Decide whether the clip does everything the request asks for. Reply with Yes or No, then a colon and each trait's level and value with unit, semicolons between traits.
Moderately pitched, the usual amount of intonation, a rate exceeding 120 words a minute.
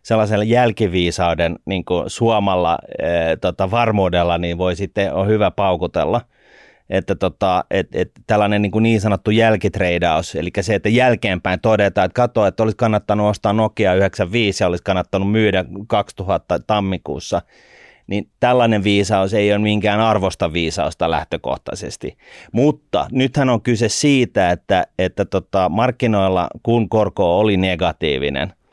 No: low, 105 Hz; average, 3.1 semitones; average, 135 wpm